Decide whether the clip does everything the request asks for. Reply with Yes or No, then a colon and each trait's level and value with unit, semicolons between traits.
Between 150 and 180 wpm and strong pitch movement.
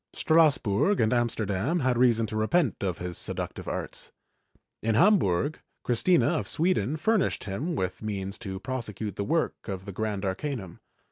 Yes: average, 160 wpm; wide, 7.6 semitones